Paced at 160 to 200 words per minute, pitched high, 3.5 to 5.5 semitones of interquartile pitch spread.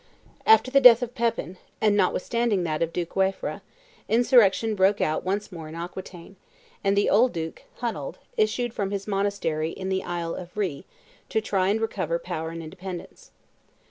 Yes: average, 170 wpm; high, 195 Hz; average, 4.3 semitones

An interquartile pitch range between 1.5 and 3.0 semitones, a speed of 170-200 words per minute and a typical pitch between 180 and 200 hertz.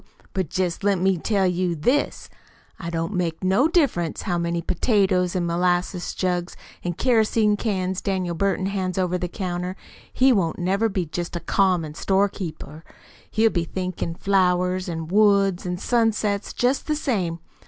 No: narrow, 2.5 semitones; average, 155 wpm; medium, 185 Hz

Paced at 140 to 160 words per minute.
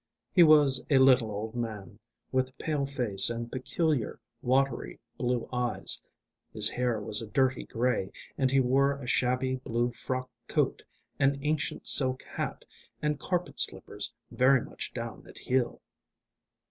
Yes: average, 145 wpm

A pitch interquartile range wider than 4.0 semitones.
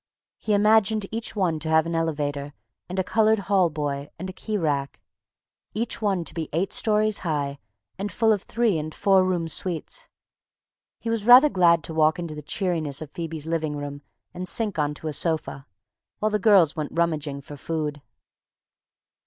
Yes: average, 5.0 semitones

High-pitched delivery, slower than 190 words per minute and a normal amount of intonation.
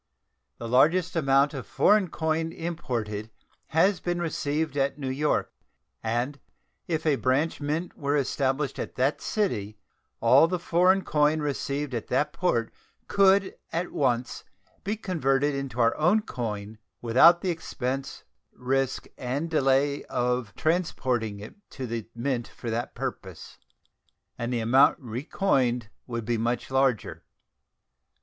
No: low, 135 Hz; slow, 135 wpm; average, 4.9 semitones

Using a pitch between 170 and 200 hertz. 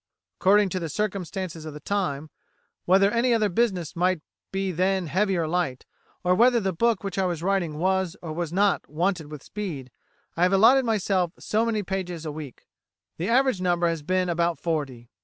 Yes: medium, 185 Hz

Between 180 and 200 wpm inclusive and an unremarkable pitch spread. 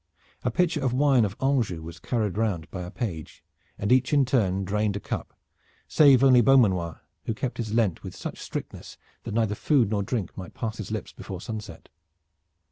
Yes: average, 190 wpm; average, 4.6 semitones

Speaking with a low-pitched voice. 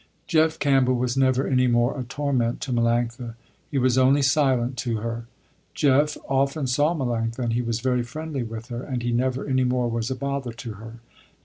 Yes: low, 125 Hz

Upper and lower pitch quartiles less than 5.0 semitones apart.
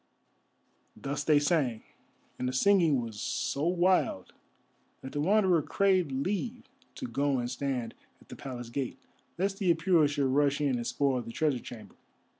No: wide, 5.6 semitones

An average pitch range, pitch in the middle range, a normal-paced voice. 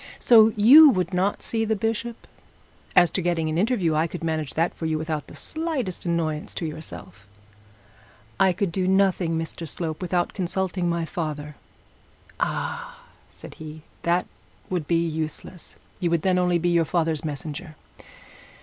Yes: average, 3.1 semitones; medium, 175 Hz; average, 160 wpm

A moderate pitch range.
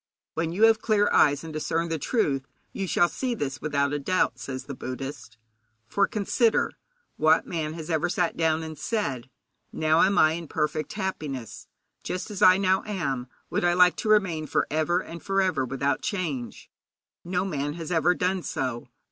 Yes: average, 4.4 semitones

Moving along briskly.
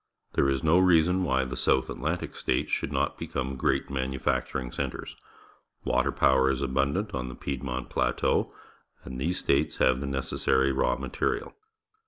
No: average, 160 wpm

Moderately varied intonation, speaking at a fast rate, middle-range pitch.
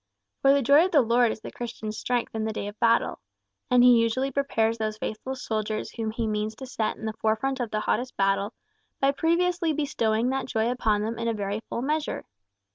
No: average, 3.5 semitones; fast, 210 wpm; high, 230 Hz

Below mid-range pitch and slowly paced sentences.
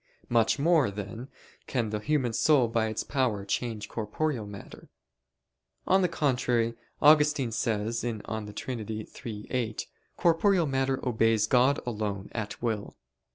Yes: low, 115 Hz; slow, 130 wpm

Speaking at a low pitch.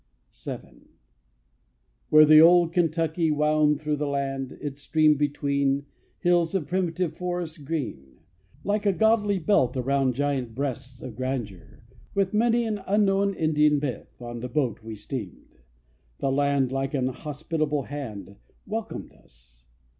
No: medium, 145 Hz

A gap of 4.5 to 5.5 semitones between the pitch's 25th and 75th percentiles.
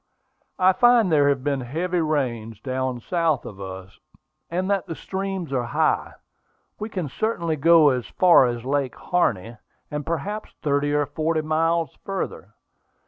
Yes: average, 5.1 semitones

